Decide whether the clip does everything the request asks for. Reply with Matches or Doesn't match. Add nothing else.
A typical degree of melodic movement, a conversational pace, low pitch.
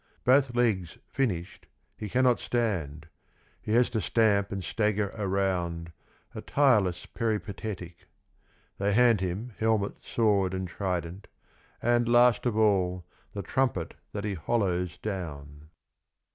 Doesn't match